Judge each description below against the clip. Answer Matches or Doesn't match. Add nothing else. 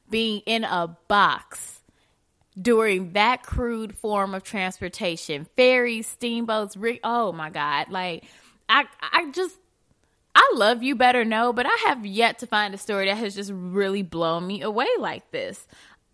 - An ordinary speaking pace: Matches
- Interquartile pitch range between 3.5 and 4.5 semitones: Matches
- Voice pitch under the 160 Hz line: Doesn't match